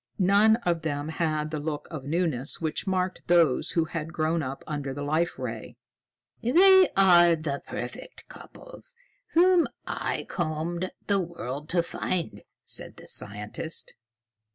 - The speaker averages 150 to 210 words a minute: No, average, 140 wpm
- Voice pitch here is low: No, medium, 165 Hz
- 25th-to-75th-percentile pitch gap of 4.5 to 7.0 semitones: No, average, 3.4 semitones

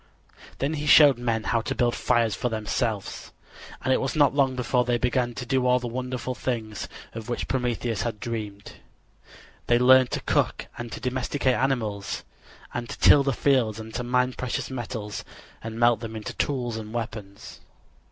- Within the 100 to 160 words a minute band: No, average, 180 wpm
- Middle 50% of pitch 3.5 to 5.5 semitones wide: No, narrow, 2.4 semitones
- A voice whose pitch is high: No, low, 120 Hz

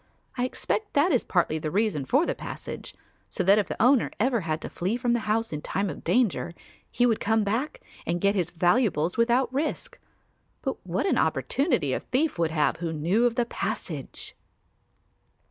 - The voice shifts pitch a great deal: Yes, wide, 6.3 semitones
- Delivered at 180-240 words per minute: Yes, average, 190 wpm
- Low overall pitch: No, high, 215 Hz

